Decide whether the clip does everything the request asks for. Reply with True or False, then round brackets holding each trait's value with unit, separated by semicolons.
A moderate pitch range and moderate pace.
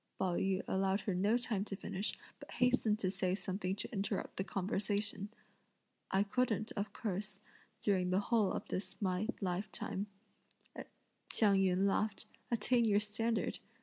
False (2.0 semitones; 150 wpm)